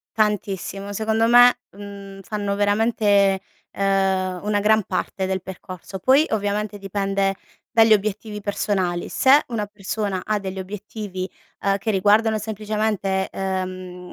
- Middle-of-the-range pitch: No, high, 200 Hz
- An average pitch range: No, narrow, 1.9 semitones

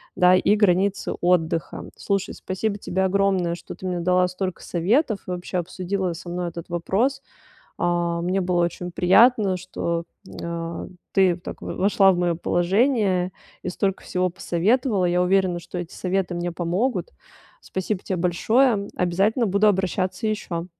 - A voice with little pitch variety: Yes, narrow, 2.2 semitones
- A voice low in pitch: No, medium, 185 Hz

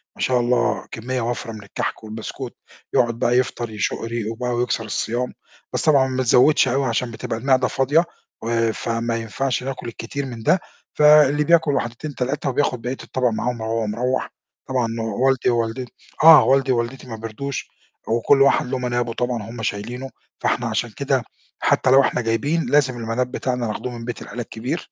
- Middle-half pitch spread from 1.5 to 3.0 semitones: Yes, narrow, 2.5 semitones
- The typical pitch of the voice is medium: No, low, 125 Hz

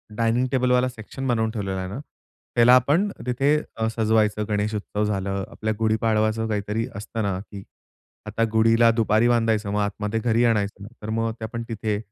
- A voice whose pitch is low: Yes, low, 110 Hz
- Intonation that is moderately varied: No, narrow, 1.9 semitones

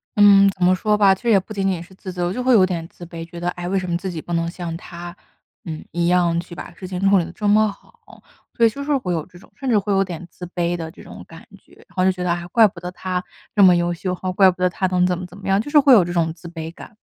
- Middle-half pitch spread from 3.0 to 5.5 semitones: No, narrow, 2.4 semitones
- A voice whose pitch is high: No, medium, 180 Hz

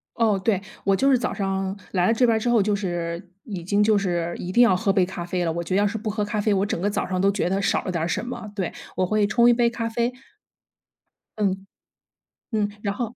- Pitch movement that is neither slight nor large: Yes, average, 3.0 semitones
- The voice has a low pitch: No, high, 200 Hz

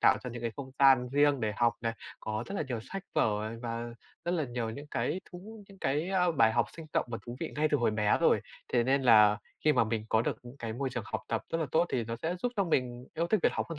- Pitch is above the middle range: No, low, 125 Hz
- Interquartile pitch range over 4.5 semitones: Yes, wide, 5.6 semitones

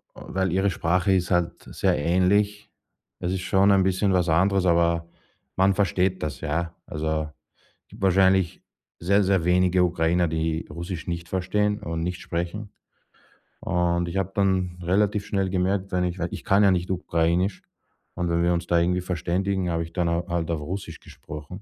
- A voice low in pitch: Yes, very low, 90 Hz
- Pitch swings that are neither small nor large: No, narrow, 2.1 semitones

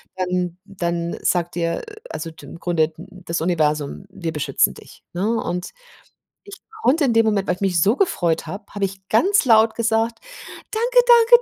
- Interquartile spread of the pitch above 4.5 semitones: Yes, average, 5.0 semitones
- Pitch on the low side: No, high, 190 Hz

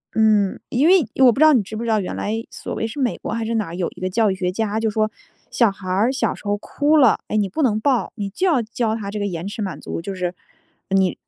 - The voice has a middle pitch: No, high, 215 Hz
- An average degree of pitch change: Yes, average, 3.2 semitones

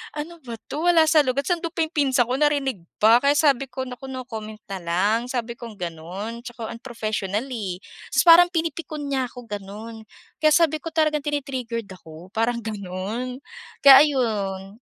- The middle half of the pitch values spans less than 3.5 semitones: No, average, 5.3 semitones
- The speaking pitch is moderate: No, high, 245 Hz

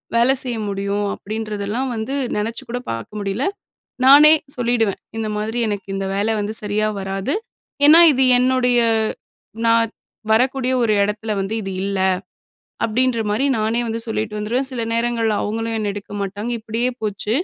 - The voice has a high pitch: Yes, high, 220 Hz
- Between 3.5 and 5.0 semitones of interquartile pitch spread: No, average, 2.7 semitones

